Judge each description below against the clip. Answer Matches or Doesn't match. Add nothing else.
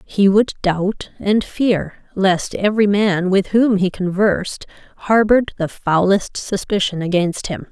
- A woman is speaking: Matches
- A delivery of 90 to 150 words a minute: Matches